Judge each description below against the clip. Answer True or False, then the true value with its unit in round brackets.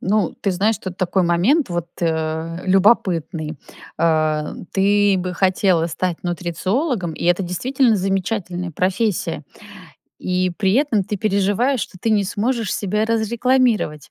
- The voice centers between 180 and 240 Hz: True (190 Hz)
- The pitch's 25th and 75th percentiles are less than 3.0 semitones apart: False (3.8 semitones)